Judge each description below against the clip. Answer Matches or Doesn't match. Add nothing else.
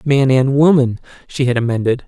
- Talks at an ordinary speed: Matches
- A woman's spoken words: Doesn't match